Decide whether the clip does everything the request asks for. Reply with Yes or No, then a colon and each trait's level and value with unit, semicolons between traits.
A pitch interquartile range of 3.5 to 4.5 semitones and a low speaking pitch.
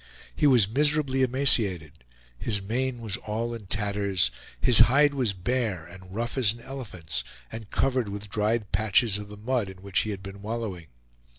Yes: average, 4.1 semitones; low, 105 Hz